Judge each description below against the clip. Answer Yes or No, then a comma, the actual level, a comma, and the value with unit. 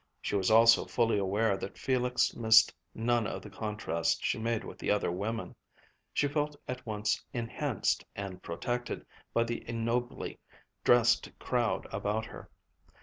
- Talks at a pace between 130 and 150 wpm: Yes, average, 145 wpm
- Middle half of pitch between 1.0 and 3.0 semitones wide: Yes, narrow, 2.6 semitones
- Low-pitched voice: Yes, low, 115 Hz